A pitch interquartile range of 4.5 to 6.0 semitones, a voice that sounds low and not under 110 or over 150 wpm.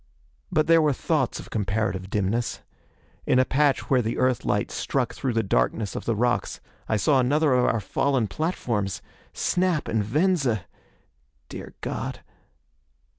Yes: wide, 5.5 semitones; low, 125 Hz; average, 145 wpm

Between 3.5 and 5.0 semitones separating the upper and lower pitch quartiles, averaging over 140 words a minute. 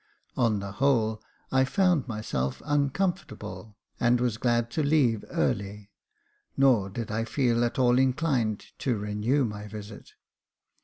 No: average, 4.1 semitones; slow, 135 wpm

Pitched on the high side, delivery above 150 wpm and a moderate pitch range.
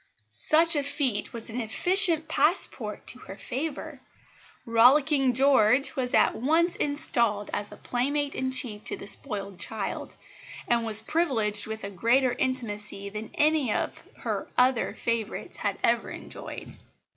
No: very high, 250 Hz; average, 140 wpm; average, 4.9 semitones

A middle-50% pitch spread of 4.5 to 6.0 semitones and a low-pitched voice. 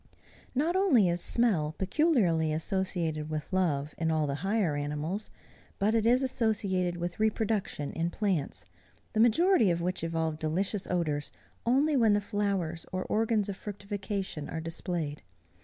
No: average, 5.1 semitones; medium, 185 Hz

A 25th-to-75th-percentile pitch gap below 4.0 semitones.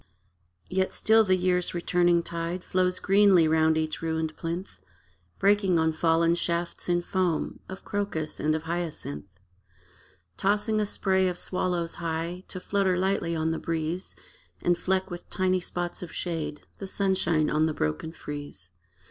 Yes: narrow, 2.6 semitones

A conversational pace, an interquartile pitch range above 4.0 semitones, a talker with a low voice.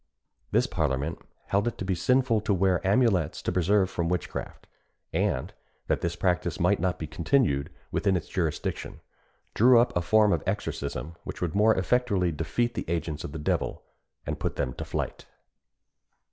Yes: average, 170 wpm; average, 4.4 semitones; very low, 90 Hz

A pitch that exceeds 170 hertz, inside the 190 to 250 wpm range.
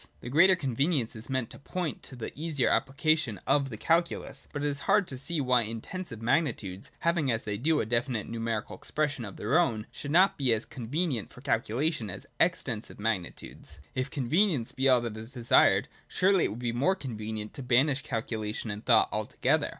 No: low, 130 Hz; average, 200 wpm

